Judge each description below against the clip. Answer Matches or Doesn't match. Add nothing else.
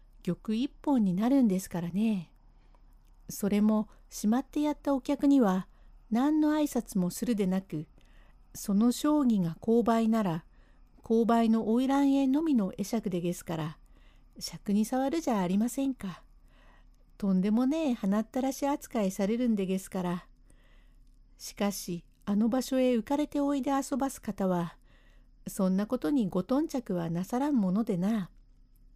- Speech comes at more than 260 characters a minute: Matches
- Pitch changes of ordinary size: Doesn't match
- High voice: Matches